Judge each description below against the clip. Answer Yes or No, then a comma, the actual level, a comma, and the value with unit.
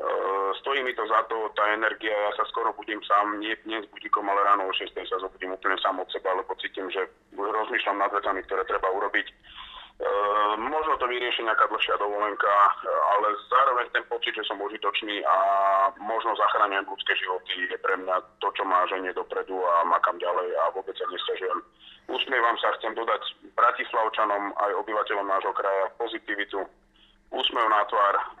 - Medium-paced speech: No, fast, 175 wpm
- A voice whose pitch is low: Yes, low, 105 Hz